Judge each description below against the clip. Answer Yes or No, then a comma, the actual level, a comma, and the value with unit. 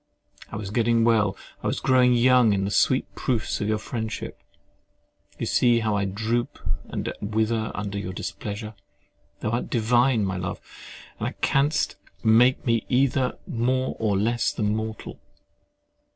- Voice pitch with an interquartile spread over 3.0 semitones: No, narrow, 2.6 semitones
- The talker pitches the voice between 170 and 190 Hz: No, low, 115 Hz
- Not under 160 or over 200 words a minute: No, average, 150 wpm